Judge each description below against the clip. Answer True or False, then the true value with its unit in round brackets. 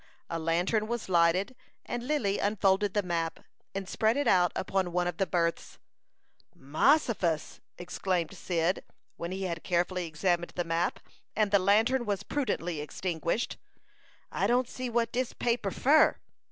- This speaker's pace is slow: False (150 wpm)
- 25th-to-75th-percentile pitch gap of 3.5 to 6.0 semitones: True (4.6 semitones)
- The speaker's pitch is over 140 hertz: True (190 Hz)